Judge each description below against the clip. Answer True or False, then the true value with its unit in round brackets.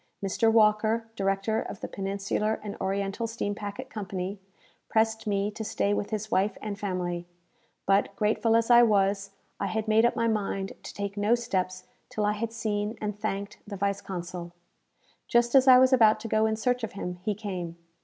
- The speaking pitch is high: True (210 Hz)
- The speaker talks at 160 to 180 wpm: False (190 wpm)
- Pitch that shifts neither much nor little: False (2.2 semitones)